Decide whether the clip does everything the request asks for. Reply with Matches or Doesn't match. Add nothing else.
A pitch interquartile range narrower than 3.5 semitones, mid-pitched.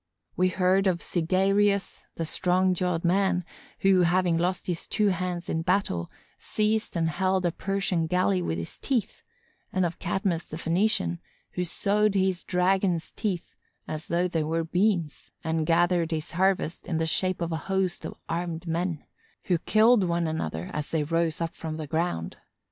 Matches